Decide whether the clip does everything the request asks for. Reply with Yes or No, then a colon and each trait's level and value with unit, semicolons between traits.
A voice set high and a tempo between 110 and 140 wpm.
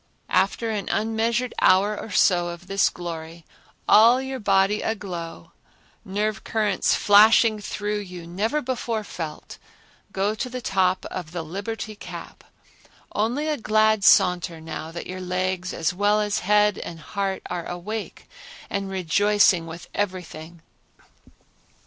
Yes: high, 200 Hz; slow, 135 wpm